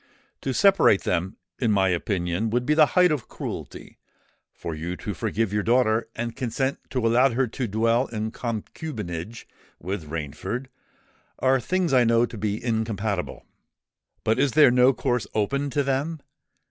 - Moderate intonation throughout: Yes, average, 4.3 semitones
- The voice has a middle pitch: No, low, 115 Hz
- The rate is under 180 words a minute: Yes, average, 160 wpm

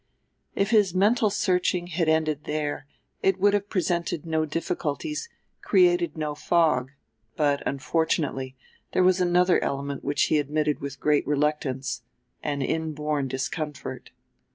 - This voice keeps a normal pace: No, slow, 130 wpm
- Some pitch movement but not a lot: Yes, average, 4.0 semitones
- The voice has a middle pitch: Yes, medium, 155 Hz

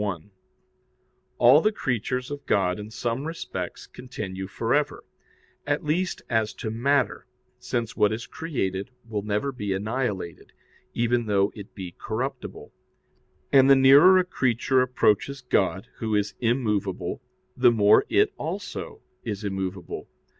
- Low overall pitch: Yes, low, 115 Hz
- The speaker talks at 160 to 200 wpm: No, slow, 135 wpm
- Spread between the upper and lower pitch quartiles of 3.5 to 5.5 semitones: Yes, average, 4.6 semitones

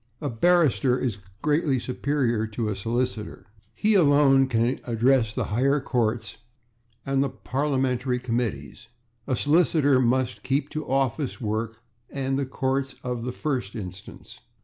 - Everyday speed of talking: No, slow, 130 wpm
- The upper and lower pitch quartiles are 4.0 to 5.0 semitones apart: No, average, 2.9 semitones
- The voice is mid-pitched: No, low, 130 Hz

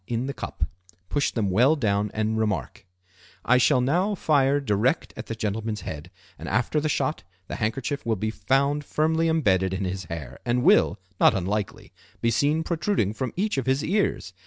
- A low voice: Yes, low, 120 Hz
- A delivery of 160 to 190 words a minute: Yes, average, 180 wpm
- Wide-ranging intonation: Yes, wide, 6.2 semitones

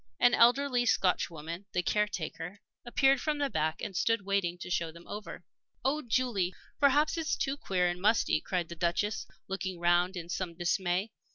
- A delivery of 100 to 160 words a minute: No, average, 175 wpm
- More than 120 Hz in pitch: Yes, high, 190 Hz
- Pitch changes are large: Yes, wide, 5.7 semitones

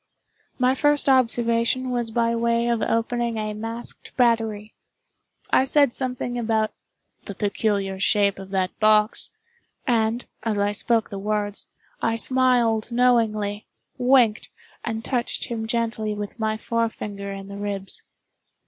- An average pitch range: No, narrow, 2.2 semitones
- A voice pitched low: No, high, 225 Hz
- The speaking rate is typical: No, slow, 130 wpm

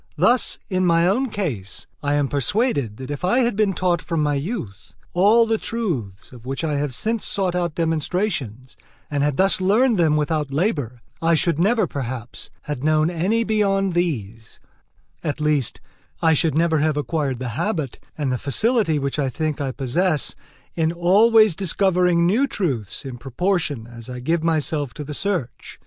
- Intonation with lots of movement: Yes, wide, 5.7 semitones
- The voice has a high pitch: No, medium, 160 Hz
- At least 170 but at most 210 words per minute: Yes, average, 175 wpm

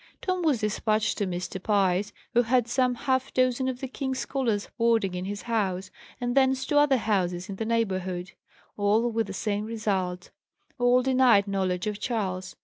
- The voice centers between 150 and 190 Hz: No, high, 220 Hz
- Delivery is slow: No, average, 175 wpm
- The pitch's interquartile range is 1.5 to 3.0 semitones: No, average, 4.6 semitones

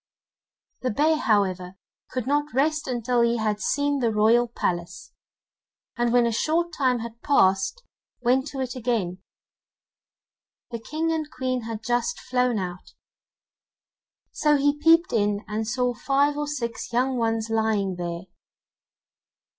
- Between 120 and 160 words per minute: Yes, average, 140 wpm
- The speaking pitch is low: No, high, 240 Hz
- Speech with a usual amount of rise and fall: Yes, average, 4.5 semitones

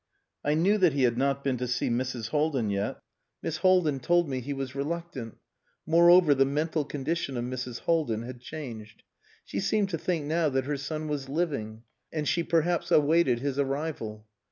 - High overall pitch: No, medium, 140 Hz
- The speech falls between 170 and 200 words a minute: Yes, average, 180 wpm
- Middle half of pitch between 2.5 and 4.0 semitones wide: No, average, 4.4 semitones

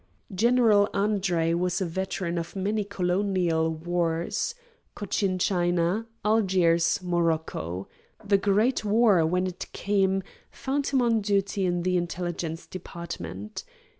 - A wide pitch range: No, average, 3.0 semitones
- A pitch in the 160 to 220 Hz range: Yes, medium, 185 Hz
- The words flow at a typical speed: No, slow, 115 wpm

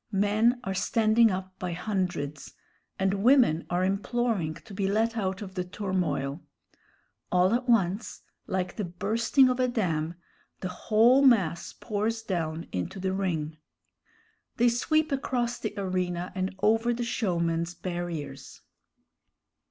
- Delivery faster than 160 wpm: No, slow, 135 wpm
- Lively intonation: No, average, 4.4 semitones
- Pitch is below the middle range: No, high, 195 Hz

